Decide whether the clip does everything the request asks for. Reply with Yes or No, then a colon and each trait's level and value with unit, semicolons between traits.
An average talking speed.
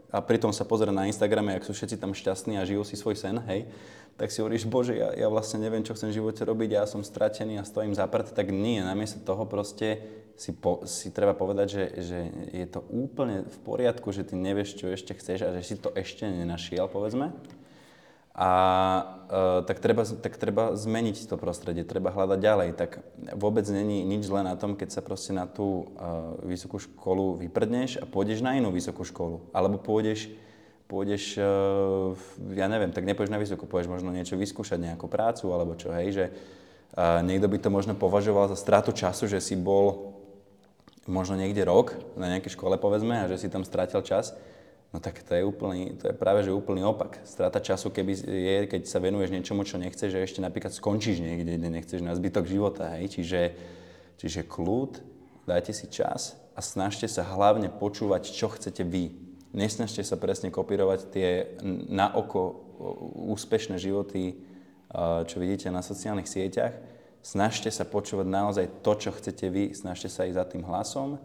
No: fast, 185 wpm